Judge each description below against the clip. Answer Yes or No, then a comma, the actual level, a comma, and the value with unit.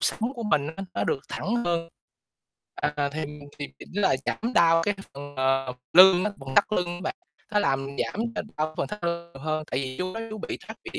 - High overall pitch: No, medium, 170 Hz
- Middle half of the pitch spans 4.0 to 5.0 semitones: No, wide, 5.4 semitones